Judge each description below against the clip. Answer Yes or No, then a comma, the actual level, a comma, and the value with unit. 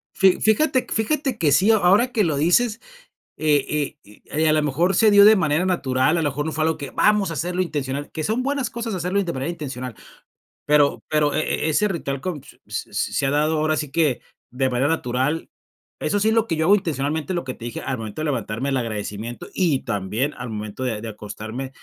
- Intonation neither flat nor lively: No, wide, 6.0 semitones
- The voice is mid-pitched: Yes, medium, 155 Hz